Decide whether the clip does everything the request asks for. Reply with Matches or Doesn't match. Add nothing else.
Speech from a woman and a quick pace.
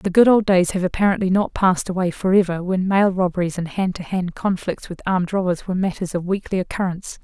Matches